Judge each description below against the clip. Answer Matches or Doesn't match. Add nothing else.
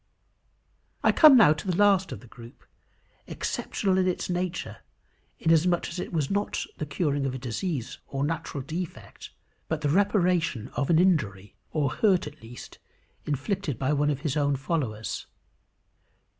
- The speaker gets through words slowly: Doesn't match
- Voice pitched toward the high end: Doesn't match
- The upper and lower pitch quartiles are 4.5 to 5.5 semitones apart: Matches